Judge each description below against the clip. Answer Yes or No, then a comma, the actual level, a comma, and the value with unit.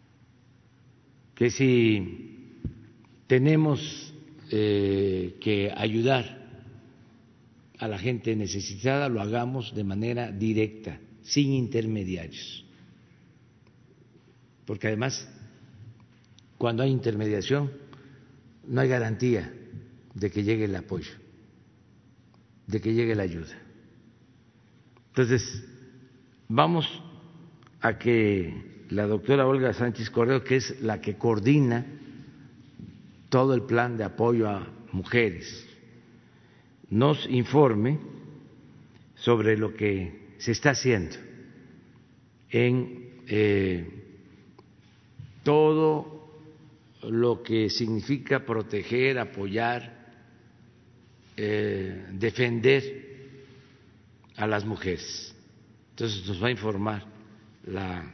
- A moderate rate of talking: No, slow, 85 wpm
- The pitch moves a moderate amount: Yes, average, 3.0 semitones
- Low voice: Yes, low, 115 Hz